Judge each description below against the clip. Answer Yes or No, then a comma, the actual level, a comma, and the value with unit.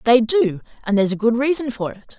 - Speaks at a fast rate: Yes, fast, 220 wpm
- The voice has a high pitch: Yes, high, 235 Hz